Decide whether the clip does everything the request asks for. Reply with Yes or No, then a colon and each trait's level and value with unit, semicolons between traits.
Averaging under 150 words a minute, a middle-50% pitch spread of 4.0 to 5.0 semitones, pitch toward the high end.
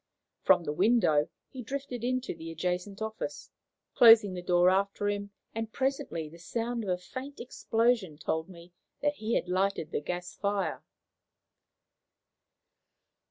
Yes: average, 140 wpm; average, 4.7 semitones; high, 200 Hz